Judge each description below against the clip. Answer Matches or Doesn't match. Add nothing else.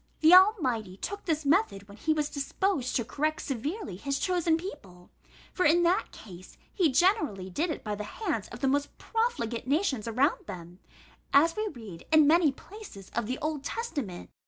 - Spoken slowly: Doesn't match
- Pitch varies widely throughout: Matches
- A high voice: Matches